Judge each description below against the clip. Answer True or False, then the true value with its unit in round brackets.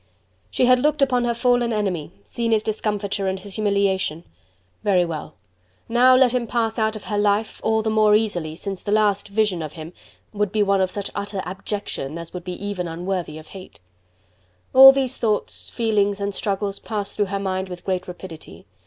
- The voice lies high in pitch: True (205 Hz)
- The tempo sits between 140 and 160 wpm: False (190 wpm)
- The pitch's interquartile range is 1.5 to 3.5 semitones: True (2.8 semitones)